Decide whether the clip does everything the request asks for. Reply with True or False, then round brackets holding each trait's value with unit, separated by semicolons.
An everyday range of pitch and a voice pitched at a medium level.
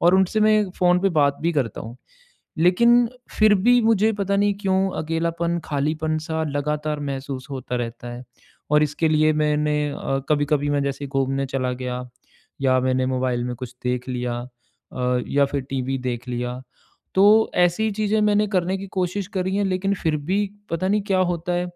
False (6.0 semitones; 155 Hz)